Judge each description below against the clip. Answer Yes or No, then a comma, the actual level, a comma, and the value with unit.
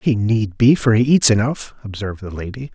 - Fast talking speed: Yes, fast, 220 wpm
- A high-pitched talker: No, low, 110 Hz